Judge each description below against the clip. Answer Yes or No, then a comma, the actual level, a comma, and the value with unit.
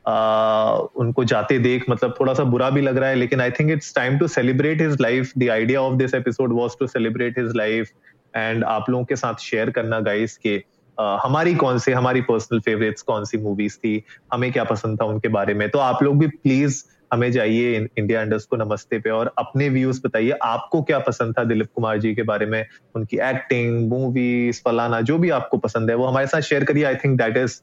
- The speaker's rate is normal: Yes, average, 175 wpm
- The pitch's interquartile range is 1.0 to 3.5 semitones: Yes, average, 2.9 semitones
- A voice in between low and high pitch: No, low, 120 Hz